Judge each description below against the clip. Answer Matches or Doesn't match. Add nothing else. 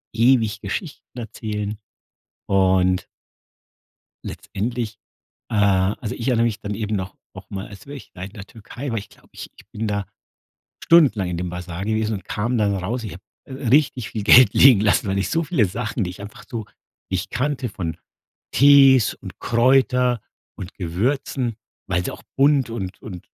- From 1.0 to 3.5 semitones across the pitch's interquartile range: Doesn't match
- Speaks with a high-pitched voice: Doesn't match